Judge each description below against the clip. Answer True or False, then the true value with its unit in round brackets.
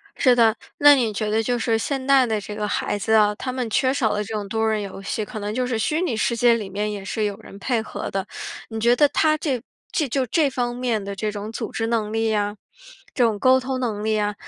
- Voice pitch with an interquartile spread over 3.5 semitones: False (3.2 semitones)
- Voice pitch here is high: True (225 Hz)